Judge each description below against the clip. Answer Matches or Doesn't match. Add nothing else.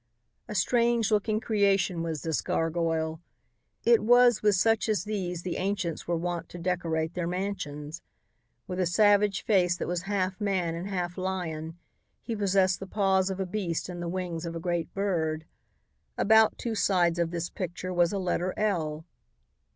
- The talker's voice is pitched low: Doesn't match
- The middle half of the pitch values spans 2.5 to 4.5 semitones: Matches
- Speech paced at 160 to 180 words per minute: Matches